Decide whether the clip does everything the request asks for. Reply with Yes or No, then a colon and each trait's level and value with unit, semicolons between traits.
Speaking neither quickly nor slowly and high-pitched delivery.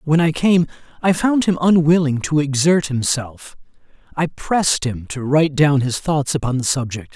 No: average, 175 wpm; medium, 150 Hz